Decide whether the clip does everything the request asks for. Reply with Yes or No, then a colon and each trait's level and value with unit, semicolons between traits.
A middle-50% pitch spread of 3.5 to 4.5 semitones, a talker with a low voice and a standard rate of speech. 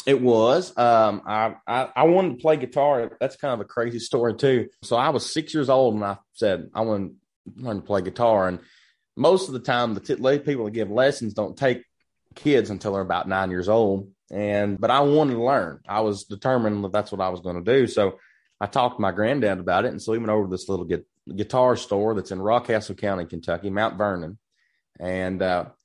No: average, 4.1 semitones; low, 110 Hz; fast, 225 wpm